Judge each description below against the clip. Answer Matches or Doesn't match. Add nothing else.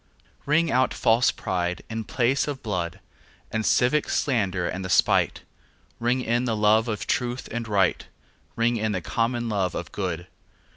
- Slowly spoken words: Doesn't match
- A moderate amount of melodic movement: Matches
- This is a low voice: Matches